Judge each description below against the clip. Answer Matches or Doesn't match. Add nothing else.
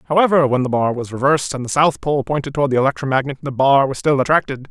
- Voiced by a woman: Doesn't match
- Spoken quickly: Matches